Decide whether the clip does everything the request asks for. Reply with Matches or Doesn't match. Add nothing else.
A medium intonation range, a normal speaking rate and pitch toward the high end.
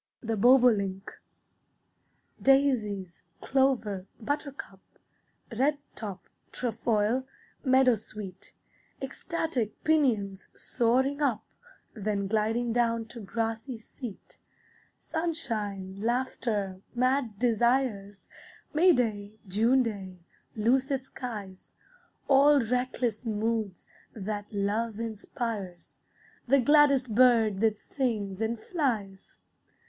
Doesn't match